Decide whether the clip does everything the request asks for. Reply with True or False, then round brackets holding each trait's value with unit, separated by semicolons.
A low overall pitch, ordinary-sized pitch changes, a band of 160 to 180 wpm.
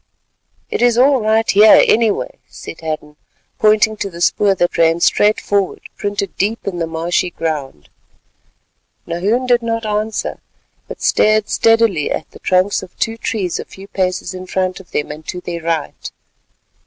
False (195 Hz; 4.2 semitones; 165 wpm)